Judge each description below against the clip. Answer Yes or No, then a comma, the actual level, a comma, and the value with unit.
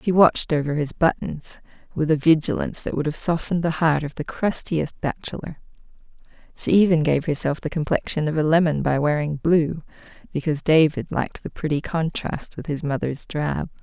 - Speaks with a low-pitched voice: No, medium, 155 Hz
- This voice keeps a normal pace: Yes, average, 175 wpm